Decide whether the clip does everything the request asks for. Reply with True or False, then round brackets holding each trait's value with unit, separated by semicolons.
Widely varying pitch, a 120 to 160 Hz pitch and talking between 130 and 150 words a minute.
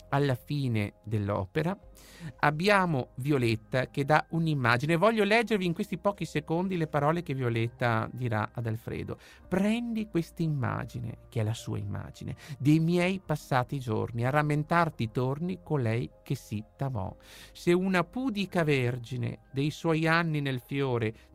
True (6.0 semitones; 140 Hz; 140 wpm)